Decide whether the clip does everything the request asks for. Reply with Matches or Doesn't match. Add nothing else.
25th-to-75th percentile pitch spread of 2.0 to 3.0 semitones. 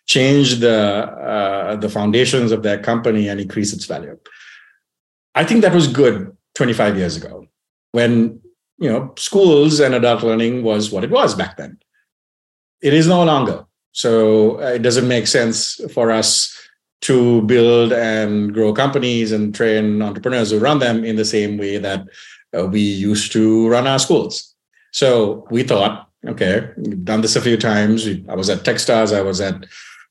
Matches